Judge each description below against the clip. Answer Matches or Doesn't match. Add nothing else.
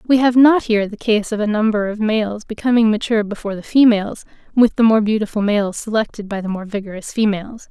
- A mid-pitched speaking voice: Doesn't match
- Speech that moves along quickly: Matches